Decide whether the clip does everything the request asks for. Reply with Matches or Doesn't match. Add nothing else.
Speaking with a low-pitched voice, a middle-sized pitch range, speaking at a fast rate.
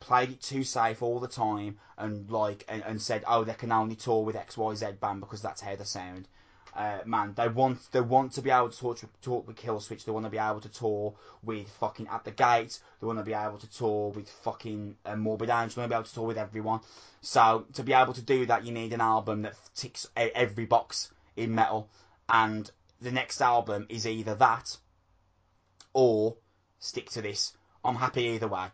Doesn't match